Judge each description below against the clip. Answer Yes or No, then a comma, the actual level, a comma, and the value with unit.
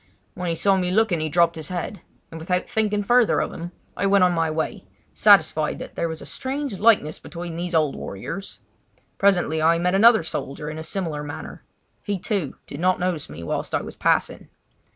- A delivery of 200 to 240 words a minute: Yes, fast, 205 wpm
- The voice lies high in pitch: No, medium, 175 Hz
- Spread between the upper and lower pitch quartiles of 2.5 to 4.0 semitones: Yes, average, 3.7 semitones